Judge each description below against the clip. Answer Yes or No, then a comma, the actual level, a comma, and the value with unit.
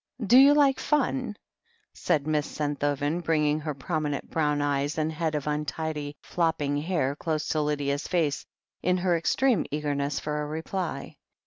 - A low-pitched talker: No, medium, 150 Hz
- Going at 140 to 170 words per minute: Yes, average, 150 wpm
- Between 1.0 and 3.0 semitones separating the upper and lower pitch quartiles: Yes, narrow, 2.6 semitones